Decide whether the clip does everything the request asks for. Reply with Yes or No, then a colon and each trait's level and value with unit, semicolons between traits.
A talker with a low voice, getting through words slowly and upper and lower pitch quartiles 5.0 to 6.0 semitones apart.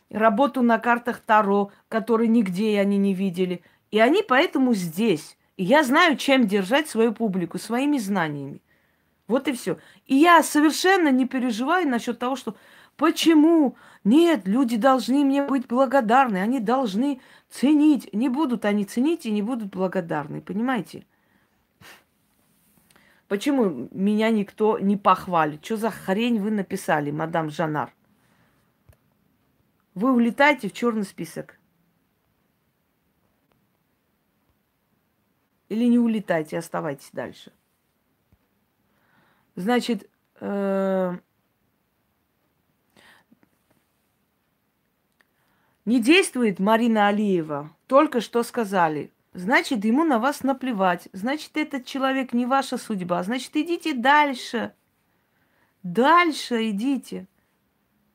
No: high, 230 Hz; slow, 100 wpm; wide, 5.5 semitones